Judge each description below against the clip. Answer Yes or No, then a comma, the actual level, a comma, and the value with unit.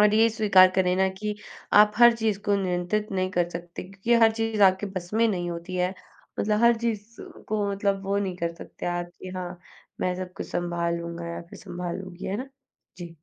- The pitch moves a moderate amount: Yes, average, 3.1 semitones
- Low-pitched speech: No, high, 190 Hz